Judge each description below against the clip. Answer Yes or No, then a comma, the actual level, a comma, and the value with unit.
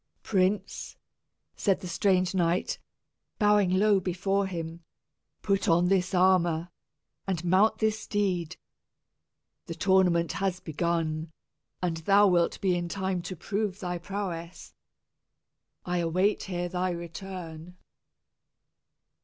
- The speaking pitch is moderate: Yes, medium, 180 Hz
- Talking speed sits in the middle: No, slow, 110 wpm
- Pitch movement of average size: No, narrow, 2.3 semitones